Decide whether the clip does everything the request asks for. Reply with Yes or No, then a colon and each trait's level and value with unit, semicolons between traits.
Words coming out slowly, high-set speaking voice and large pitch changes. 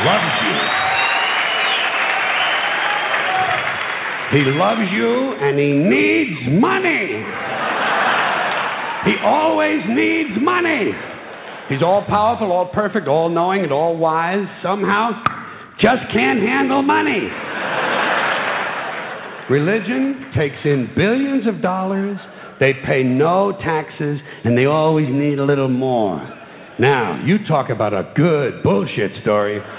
No: slow, 105 wpm; medium, 180 Hz; wide, 7.6 semitones